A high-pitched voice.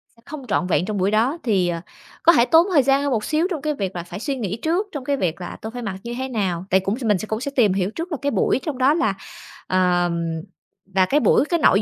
Yes: high, 230 Hz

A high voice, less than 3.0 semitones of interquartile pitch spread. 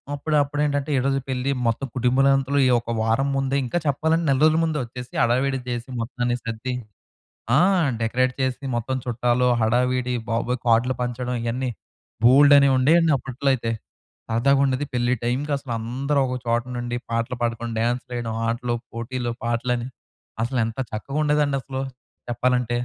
No: low, 125 Hz; narrow, 2.5 semitones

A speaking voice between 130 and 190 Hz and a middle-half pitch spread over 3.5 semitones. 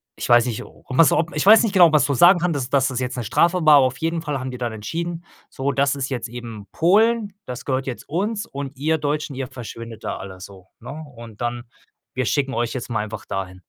Yes: low, 135 Hz; average, 5.3 semitones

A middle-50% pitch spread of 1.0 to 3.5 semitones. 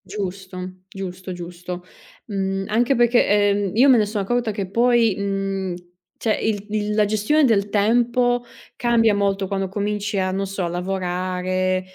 Yes: narrow, 2.6 semitones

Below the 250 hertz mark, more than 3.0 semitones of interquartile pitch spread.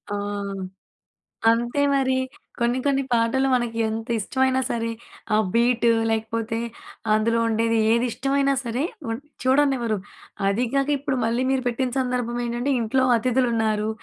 No: high, 240 Hz; narrow, 2.4 semitones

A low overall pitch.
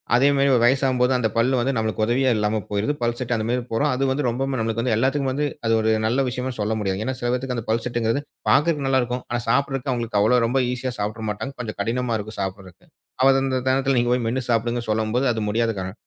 Yes: low, 120 Hz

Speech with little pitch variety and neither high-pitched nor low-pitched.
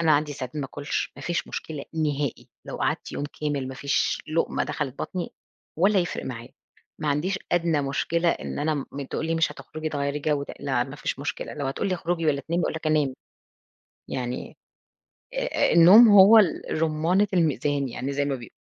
No: average, 3.1 semitones; medium, 150 Hz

